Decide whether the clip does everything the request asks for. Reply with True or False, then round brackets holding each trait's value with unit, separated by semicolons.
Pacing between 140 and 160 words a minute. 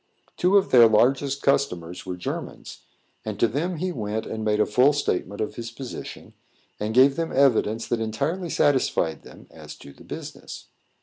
False (175 wpm)